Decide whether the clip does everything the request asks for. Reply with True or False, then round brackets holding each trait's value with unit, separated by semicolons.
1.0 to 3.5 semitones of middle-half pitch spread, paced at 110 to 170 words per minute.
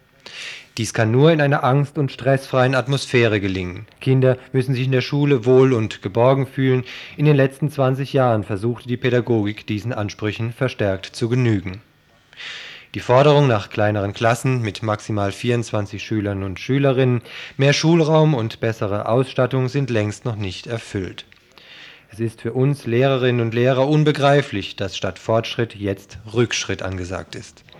False (4.0 semitones; 150 wpm)